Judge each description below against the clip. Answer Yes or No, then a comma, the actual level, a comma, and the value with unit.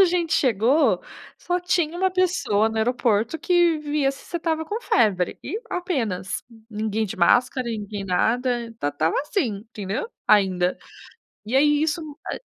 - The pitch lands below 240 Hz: No, very high, 250 Hz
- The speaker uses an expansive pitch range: Yes, wide, 7.8 semitones